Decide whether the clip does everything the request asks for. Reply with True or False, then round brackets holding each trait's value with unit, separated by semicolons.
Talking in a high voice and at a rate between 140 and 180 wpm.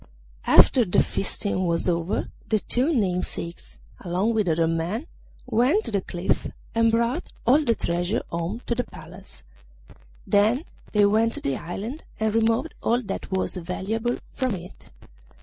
True (210 Hz; 150 wpm)